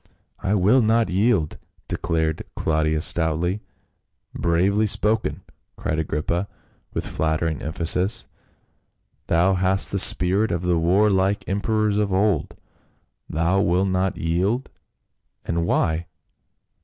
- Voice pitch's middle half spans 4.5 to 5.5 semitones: No, average, 3.6 semitones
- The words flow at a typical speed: No, slow, 125 wpm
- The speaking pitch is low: Yes, very low, 90 Hz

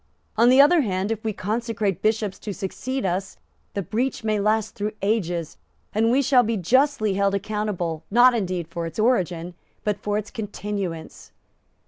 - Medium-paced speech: Yes, average, 165 wpm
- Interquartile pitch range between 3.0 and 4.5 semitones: Yes, average, 3.3 semitones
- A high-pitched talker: Yes, high, 210 Hz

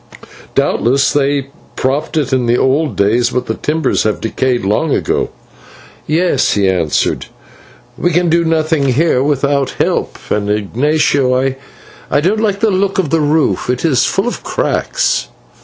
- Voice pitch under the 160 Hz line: Yes, medium, 140 Hz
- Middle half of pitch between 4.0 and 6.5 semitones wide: Yes, average, 4.3 semitones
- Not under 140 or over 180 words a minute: Yes, average, 155 wpm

